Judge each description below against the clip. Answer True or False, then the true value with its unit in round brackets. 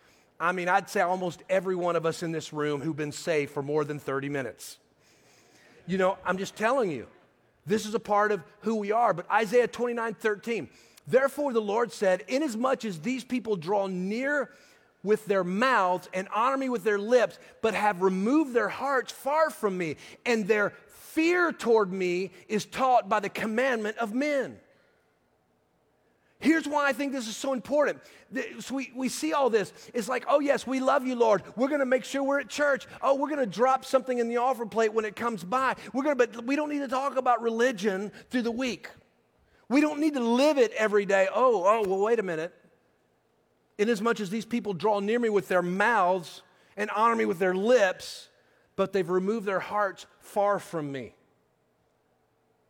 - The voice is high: True (225 Hz)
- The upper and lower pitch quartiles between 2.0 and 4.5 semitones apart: False (5.3 semitones)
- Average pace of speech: True (195 wpm)